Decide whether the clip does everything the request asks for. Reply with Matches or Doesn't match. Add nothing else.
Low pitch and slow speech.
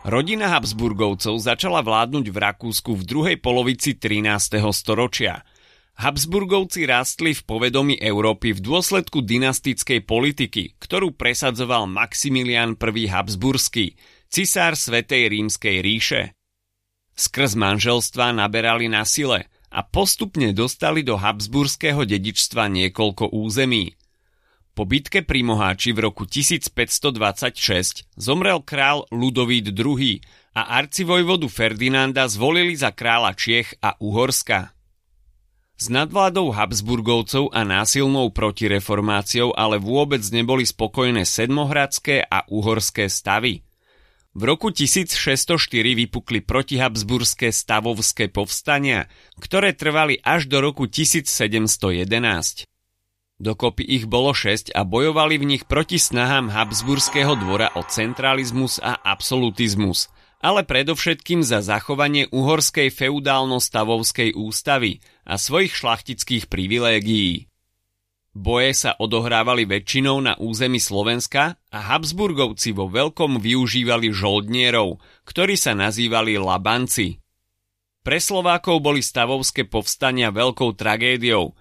Matches